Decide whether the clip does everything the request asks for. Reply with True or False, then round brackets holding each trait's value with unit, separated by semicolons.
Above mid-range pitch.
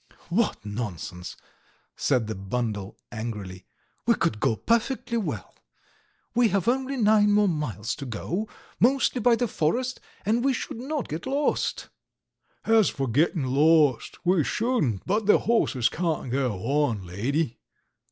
False (155 Hz)